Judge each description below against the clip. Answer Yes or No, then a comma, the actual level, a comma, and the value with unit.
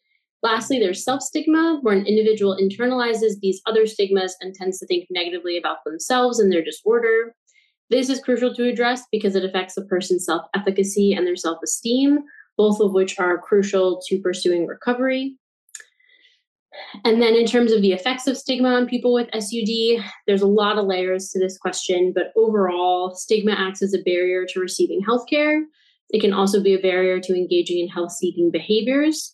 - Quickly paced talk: No, average, 175 wpm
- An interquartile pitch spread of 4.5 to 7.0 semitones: Yes, average, 4.8 semitones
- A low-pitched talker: No, high, 205 Hz